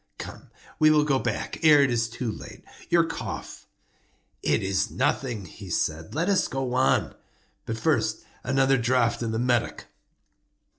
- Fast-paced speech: No, average, 155 wpm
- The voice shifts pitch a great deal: No, average, 4.1 semitones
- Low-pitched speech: Yes, low, 125 Hz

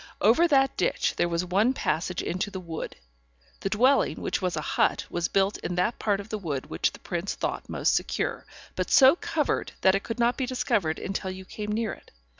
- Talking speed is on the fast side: Yes, fast, 215 wpm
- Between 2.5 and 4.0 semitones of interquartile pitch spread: No, average, 4.7 semitones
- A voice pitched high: Yes, high, 195 Hz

